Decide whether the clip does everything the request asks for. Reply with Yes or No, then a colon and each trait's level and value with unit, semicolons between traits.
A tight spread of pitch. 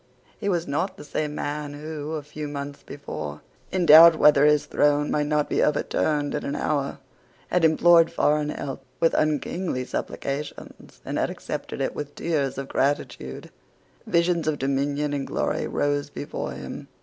Yes: narrow, 1.6 semitones